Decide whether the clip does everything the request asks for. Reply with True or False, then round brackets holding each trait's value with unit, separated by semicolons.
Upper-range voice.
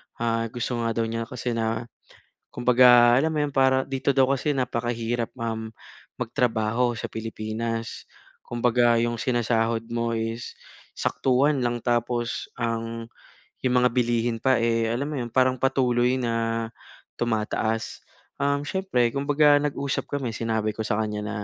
False (120 Hz)